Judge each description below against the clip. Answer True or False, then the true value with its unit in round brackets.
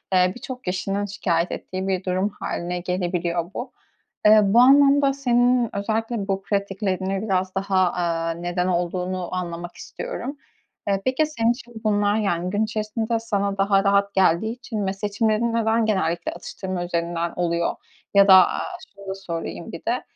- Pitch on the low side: False (195 Hz)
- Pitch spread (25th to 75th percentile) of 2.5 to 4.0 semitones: True (3.4 semitones)